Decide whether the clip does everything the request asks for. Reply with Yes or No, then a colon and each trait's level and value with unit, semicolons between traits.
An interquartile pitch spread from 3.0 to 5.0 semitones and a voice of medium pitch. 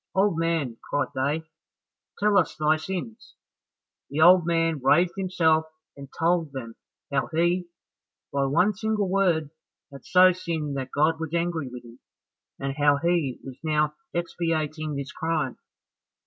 Yes: average, 3.5 semitones; medium, 160 Hz